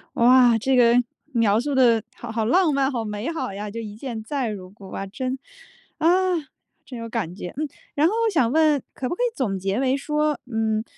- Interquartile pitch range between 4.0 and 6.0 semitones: Yes, average, 4.3 semitones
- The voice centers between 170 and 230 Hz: No, high, 240 Hz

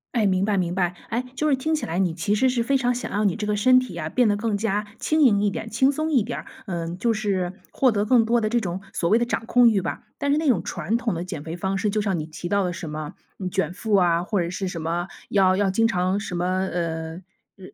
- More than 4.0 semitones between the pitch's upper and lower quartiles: Yes, average, 4.5 semitones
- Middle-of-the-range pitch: No, high, 200 Hz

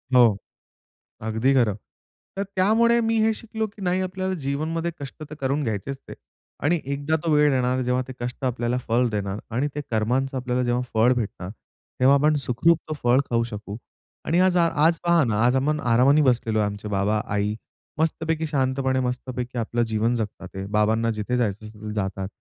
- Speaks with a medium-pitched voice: No, low, 125 Hz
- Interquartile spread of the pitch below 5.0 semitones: No, wide, 5.4 semitones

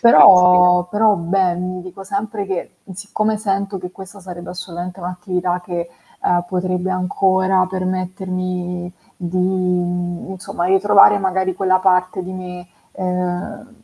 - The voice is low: No, medium, 185 Hz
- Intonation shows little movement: Yes, narrow, 1.1 semitones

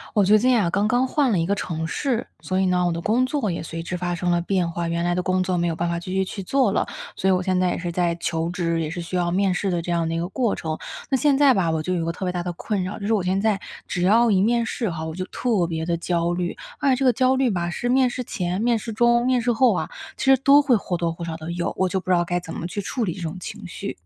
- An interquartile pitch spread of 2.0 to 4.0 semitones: No, average, 4.7 semitones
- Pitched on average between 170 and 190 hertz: Yes, medium, 185 Hz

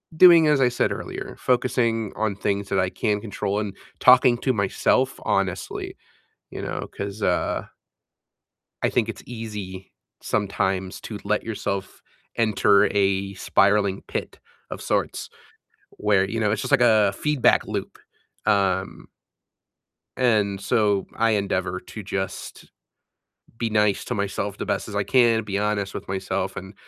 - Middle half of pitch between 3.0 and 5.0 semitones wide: No, narrow, 2.5 semitones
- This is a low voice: Yes, low, 100 Hz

